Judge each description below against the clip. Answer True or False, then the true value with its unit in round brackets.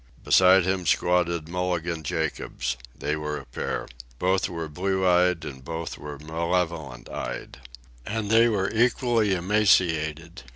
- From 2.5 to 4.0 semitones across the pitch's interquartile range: True (3.2 semitones)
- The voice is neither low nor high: False (85 Hz)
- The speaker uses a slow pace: True (130 wpm)